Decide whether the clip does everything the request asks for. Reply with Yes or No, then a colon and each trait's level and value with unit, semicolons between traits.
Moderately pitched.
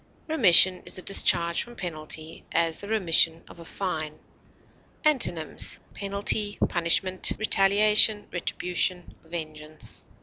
Yes: medium, 180 Hz